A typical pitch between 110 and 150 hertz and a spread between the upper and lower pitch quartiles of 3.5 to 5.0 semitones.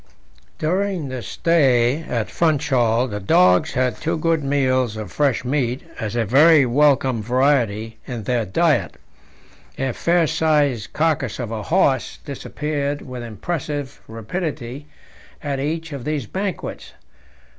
Yes: low, 135 Hz; average, 4.4 semitones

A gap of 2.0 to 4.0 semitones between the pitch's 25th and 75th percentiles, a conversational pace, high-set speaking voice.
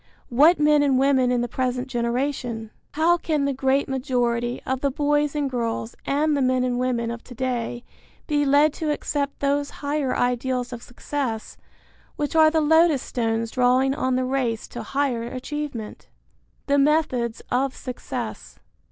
Yes: average, 2.9 semitones; average, 160 wpm; very high, 260 Hz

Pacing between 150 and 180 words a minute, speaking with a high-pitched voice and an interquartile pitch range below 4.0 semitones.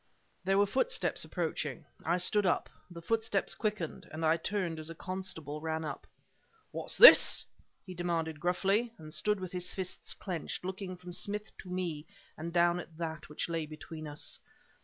No: average, 170 wpm; medium, 175 Hz; average, 3.1 semitones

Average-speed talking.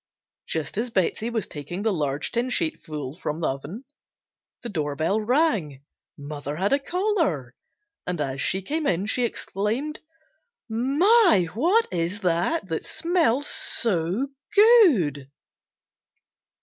No: slow, 130 wpm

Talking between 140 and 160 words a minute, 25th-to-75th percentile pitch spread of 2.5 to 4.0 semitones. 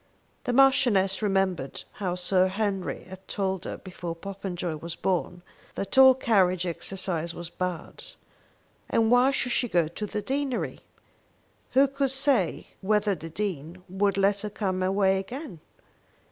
Yes: average, 145 wpm; average, 3.6 semitones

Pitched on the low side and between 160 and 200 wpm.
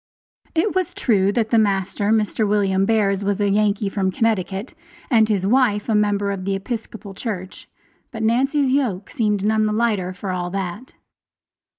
No: high, 210 Hz; average, 170 wpm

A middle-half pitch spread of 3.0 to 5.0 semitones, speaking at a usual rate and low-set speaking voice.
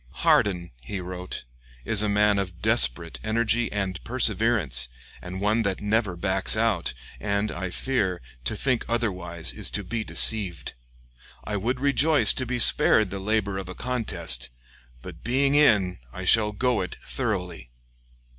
Yes: average, 4.0 semitones; average, 150 wpm; low, 100 Hz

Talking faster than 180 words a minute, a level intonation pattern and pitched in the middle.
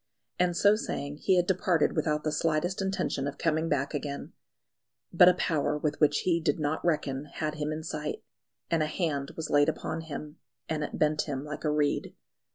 Yes: average, 195 wpm; narrow, 2.2 semitones; medium, 155 Hz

